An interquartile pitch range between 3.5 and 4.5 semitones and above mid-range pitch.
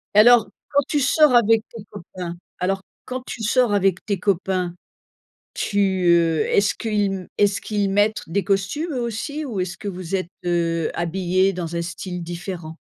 Yes: average, 3.8 semitones; high, 195 Hz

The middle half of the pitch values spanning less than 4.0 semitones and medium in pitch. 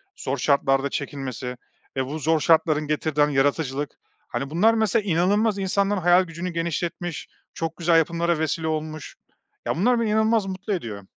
No: average, 4.3 semitones; medium, 165 Hz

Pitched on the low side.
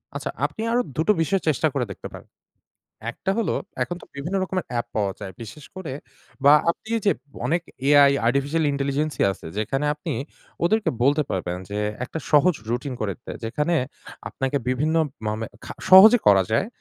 No: medium, 145 Hz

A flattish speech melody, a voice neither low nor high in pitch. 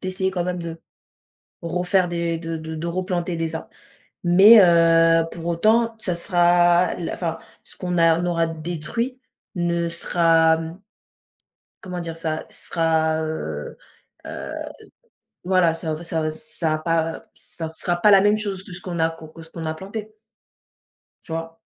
Yes: narrow, 1.8 semitones; medium, 170 Hz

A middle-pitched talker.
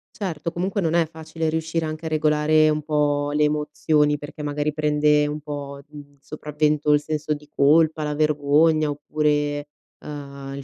Yes: medium, 150 Hz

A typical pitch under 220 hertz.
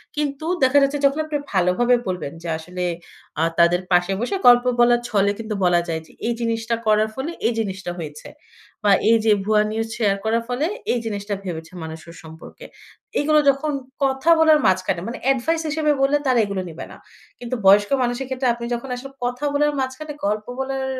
No: high, 235 Hz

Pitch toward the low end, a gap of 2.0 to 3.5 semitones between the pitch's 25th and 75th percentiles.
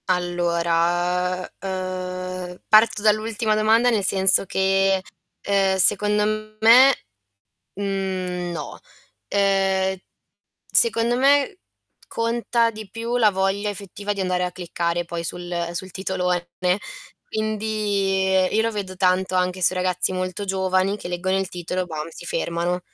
No: high, 190 Hz; narrow, 2.5 semitones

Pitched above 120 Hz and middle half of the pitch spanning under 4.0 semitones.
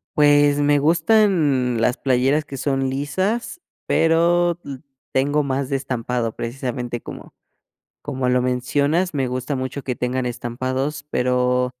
Yes: low, 135 Hz; average, 2.7 semitones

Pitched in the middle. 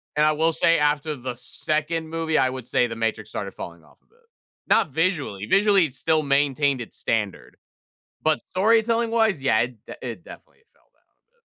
Yes: medium, 150 Hz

